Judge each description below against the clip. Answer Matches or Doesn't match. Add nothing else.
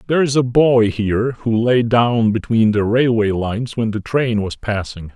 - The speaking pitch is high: Doesn't match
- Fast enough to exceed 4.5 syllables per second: Doesn't match